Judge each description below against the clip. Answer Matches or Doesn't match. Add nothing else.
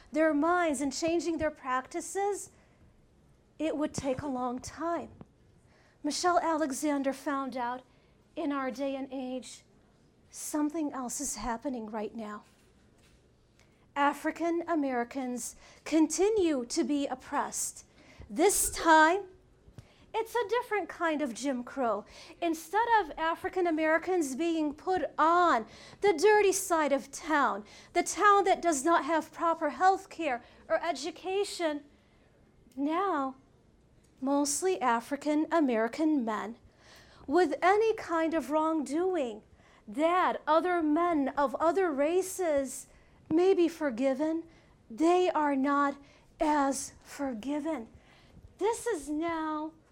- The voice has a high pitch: Matches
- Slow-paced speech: Matches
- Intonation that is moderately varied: Matches